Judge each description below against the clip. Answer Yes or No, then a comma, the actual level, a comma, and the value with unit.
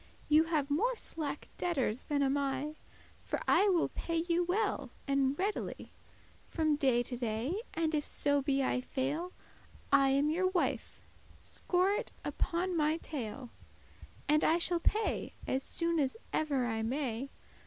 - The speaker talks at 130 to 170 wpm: Yes, average, 155 wpm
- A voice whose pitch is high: Yes, very high, 295 Hz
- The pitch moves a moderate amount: Yes, average, 4.0 semitones